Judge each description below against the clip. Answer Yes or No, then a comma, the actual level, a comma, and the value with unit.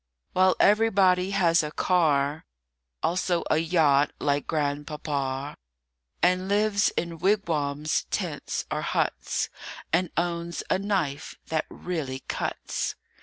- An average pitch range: Yes, average, 3.9 semitones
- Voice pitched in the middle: Yes, medium, 170 Hz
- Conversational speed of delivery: No, slow, 110 wpm